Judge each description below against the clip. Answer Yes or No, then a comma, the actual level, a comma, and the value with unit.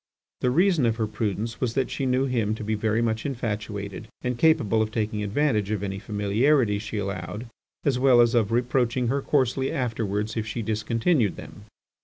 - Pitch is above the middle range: No, low, 115 Hz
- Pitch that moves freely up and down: No, average, 3.1 semitones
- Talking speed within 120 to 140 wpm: No, average, 185 wpm